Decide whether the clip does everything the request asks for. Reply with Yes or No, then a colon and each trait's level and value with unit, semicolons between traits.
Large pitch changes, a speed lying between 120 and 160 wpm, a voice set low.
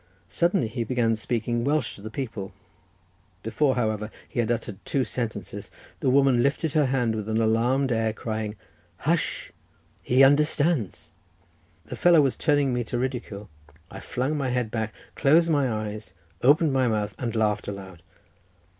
No: average, 4.0 semitones; average, 155 wpm; low, 120 Hz